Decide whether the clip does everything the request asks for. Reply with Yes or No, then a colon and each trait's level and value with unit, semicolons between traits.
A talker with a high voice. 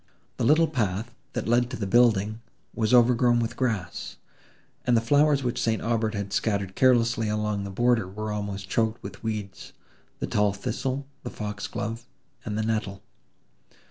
No: low, 110 Hz